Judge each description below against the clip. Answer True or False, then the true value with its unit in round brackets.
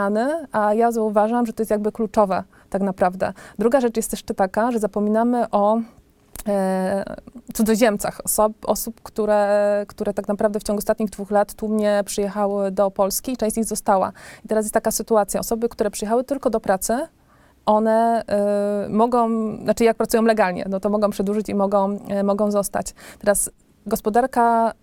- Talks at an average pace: False (165 wpm)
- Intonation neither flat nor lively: False (1.8 semitones)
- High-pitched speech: True (215 Hz)